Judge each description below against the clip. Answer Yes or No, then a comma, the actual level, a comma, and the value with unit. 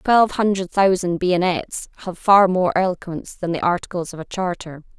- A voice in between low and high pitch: Yes, medium, 180 Hz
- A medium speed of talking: Yes, average, 170 wpm